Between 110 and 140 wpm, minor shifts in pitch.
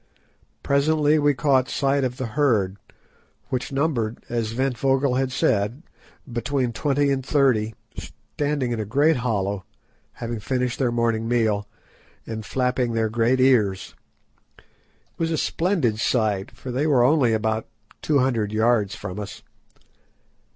No: slow, 135 wpm; average, 3.8 semitones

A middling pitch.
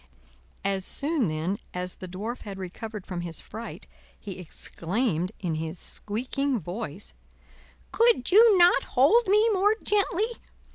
No: high, 220 Hz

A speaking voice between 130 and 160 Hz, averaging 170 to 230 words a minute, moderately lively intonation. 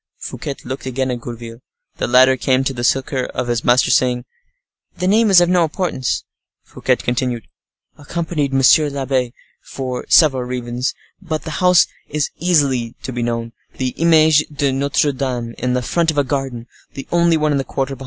Yes: low, 135 Hz; average, 175 wpm; average, 3.5 semitones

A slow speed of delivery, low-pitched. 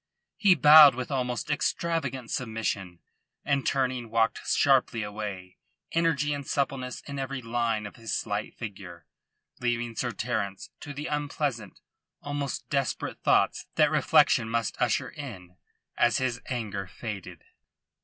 Yes: slow, 130 wpm; low, 120 Hz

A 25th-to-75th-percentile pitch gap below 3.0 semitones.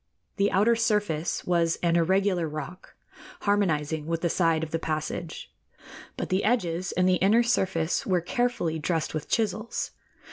No: average, 3.8 semitones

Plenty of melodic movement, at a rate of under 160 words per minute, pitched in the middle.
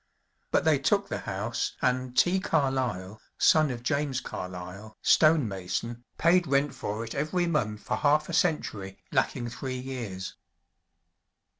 No: wide, 6.2 semitones; average, 140 wpm; low, 130 Hz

